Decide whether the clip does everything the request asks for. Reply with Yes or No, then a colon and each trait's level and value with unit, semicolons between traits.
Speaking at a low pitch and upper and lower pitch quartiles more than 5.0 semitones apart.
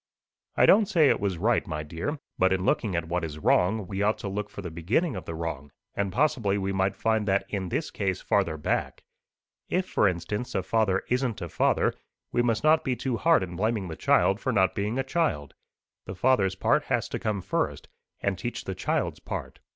No: low, 100 Hz; average, 4.6 semitones